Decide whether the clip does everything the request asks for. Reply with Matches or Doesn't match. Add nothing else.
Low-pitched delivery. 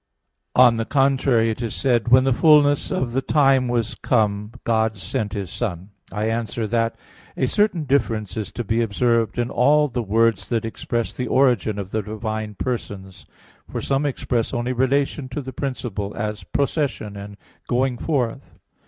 Matches